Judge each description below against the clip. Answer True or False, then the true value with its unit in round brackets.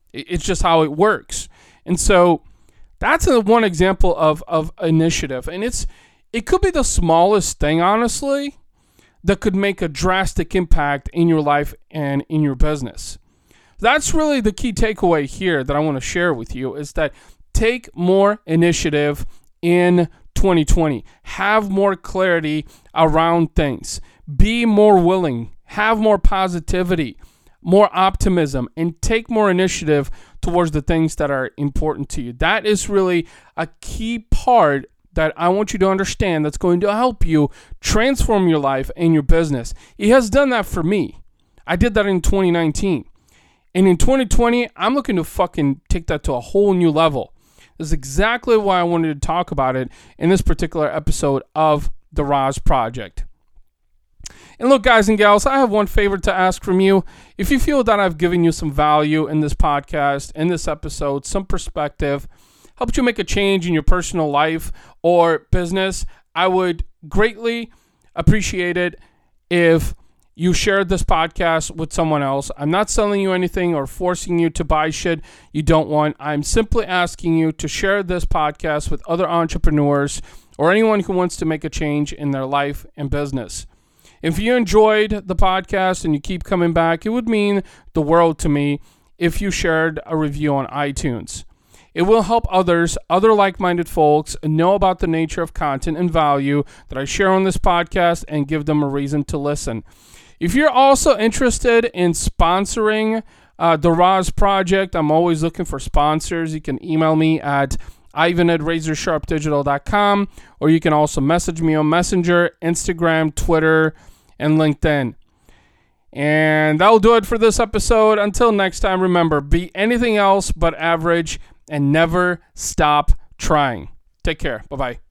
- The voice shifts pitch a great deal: False (4.4 semitones)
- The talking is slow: False (165 wpm)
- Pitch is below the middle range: False (170 Hz)